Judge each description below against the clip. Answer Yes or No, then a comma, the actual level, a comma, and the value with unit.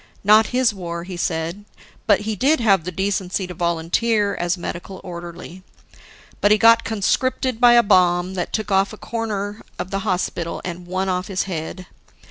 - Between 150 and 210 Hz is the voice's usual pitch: Yes, high, 190 Hz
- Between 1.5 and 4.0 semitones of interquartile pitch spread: Yes, average, 3.4 semitones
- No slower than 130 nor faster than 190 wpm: Yes, average, 170 wpm